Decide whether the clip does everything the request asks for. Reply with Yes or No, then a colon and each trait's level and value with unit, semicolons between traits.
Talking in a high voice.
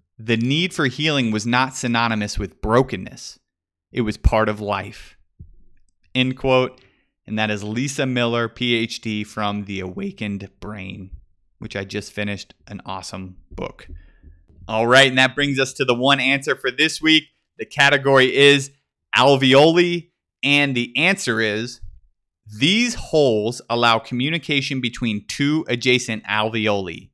No: low, 115 Hz